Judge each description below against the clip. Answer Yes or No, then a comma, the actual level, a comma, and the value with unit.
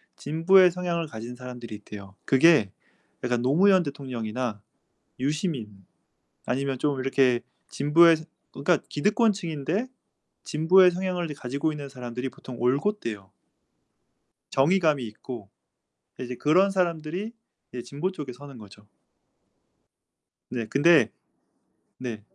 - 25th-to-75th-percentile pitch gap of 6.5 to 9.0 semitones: No, wide, 5.6 semitones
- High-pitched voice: No, medium, 140 Hz